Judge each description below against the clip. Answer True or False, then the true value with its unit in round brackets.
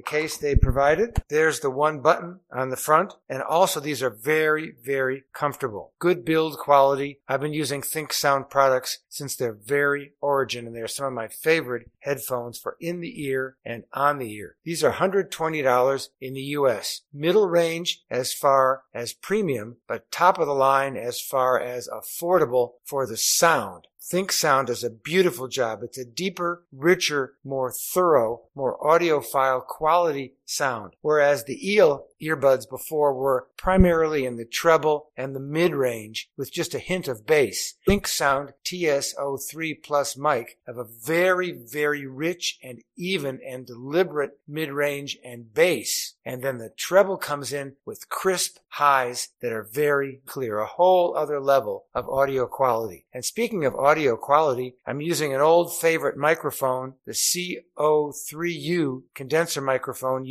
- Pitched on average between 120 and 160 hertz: True (140 Hz)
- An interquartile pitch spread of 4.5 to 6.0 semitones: False (3.7 semitones)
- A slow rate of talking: False (155 wpm)